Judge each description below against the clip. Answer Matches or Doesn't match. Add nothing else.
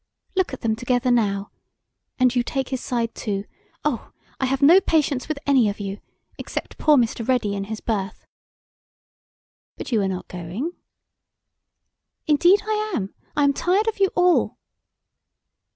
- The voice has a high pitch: Matches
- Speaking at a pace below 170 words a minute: Matches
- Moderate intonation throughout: Doesn't match